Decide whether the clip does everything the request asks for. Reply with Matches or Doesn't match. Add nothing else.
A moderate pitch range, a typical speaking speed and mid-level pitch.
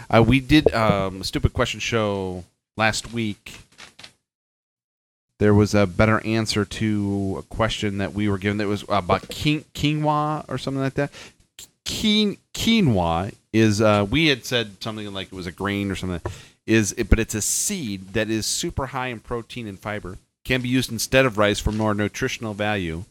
Doesn't match